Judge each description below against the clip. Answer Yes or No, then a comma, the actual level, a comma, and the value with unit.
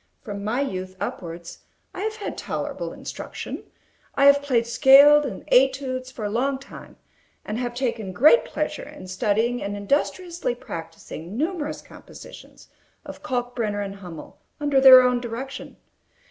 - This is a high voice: Yes, high, 245 Hz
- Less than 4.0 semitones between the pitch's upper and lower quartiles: No, average, 5.2 semitones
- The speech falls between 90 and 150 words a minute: Yes, average, 145 wpm